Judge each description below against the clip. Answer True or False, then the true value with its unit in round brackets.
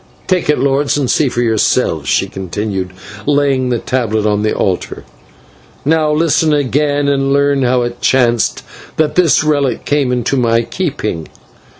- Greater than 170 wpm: False (155 wpm)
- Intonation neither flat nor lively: True (3.9 semitones)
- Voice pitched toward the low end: True (130 Hz)